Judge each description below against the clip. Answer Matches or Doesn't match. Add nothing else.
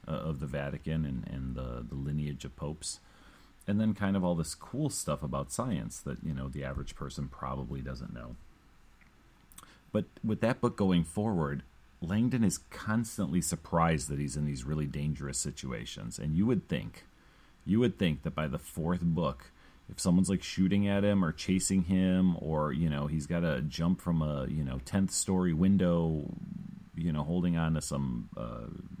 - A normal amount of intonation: Matches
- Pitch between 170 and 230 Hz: Doesn't match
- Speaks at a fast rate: Doesn't match